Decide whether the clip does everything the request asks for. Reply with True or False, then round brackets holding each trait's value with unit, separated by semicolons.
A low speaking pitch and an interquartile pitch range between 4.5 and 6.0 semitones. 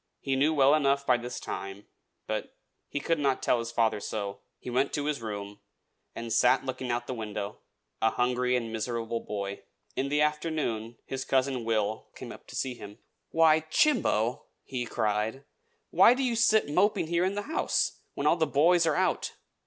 True (130 Hz; 5.1 semitones)